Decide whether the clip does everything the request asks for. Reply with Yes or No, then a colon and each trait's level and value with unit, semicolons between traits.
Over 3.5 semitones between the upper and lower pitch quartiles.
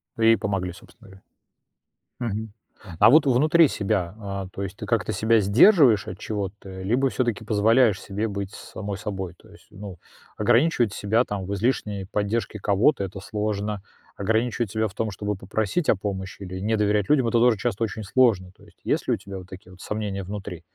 No: average, 2.7 semitones